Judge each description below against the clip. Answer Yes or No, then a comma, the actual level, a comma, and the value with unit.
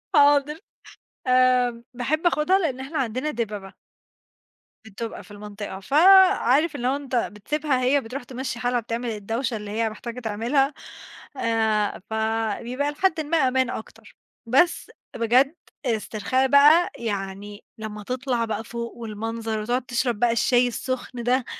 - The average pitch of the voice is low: No, high, 245 Hz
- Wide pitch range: No, average, 3.6 semitones